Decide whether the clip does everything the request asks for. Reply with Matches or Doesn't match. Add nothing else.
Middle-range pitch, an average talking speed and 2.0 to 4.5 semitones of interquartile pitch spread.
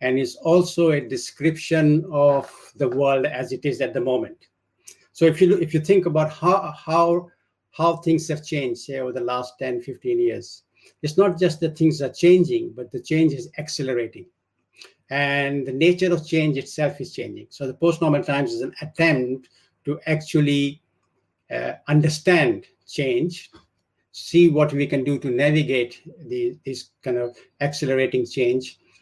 Doesn't match